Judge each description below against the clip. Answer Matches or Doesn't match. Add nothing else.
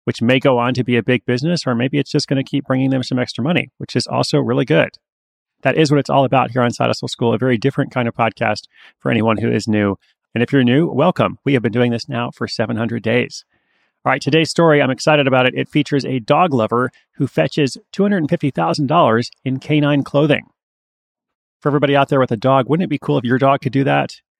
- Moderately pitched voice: Doesn't match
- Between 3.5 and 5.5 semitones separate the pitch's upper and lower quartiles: Doesn't match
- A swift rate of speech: Matches